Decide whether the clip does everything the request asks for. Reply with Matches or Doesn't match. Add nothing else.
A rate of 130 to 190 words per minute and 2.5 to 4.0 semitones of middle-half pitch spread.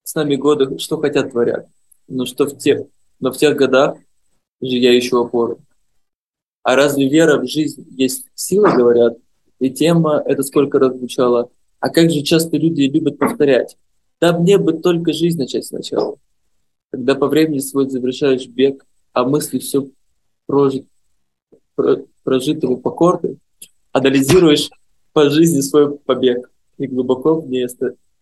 Matches